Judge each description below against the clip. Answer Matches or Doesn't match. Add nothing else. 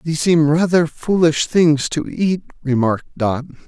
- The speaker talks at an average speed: Matches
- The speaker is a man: Matches